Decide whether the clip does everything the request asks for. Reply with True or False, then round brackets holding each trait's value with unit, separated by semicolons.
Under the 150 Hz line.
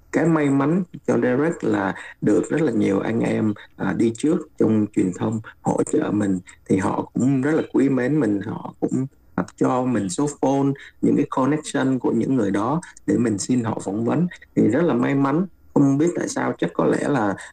True (135 Hz)